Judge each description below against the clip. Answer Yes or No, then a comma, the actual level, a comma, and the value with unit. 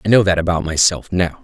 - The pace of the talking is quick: Yes, fast, 250 wpm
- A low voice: Yes, very low, 90 Hz